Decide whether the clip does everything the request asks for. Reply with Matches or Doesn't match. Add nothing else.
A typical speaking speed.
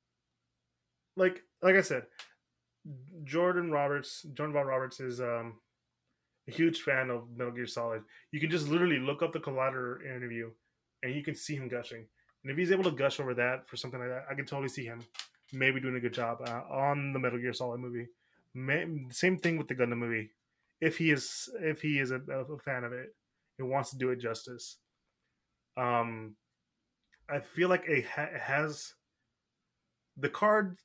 Matches